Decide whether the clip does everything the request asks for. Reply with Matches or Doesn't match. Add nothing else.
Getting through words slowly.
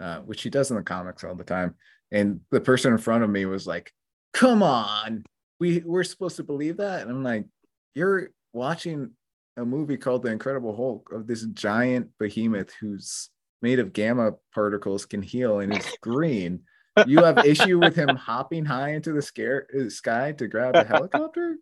Doesn't match